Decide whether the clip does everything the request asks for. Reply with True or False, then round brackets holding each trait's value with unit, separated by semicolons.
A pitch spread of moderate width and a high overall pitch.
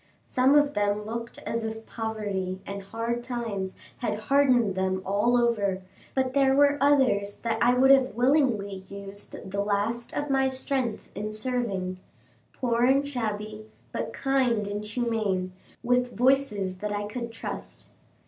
True (4.0 semitones; 230 Hz)